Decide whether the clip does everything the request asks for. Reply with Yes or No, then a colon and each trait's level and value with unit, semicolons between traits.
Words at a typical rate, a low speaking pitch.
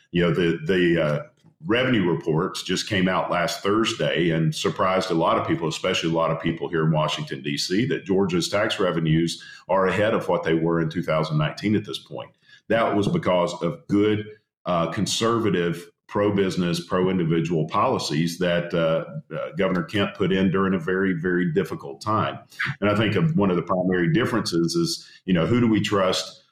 Yes: average, 185 wpm; very low, 85 Hz